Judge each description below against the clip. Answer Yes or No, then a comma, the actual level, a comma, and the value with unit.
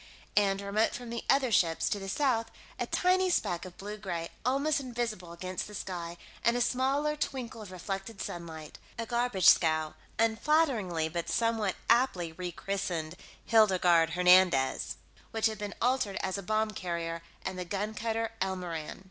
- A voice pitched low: No, high, 200 Hz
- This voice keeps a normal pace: Yes, average, 155 wpm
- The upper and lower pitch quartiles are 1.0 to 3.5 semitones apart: No, average, 4.7 semitones